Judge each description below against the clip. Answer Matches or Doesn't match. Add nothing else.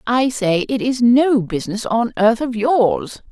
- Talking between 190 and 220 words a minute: Doesn't match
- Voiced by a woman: Matches